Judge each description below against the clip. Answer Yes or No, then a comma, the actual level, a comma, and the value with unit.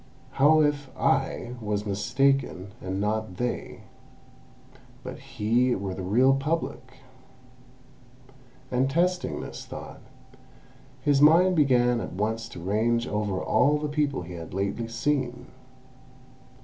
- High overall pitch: No, low, 125 Hz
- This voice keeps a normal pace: No, slow, 120 wpm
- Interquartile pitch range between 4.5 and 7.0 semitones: Yes, average, 5.0 semitones